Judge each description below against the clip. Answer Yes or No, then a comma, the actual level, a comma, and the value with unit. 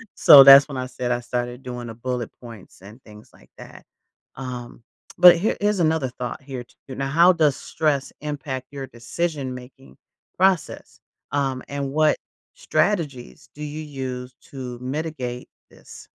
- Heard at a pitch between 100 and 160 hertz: Yes, low, 135 Hz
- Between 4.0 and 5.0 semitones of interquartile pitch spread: No, average, 3.4 semitones